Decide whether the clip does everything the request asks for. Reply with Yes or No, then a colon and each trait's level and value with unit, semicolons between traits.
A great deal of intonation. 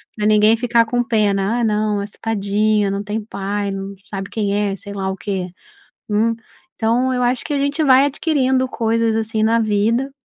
No: average, 3.0 semitones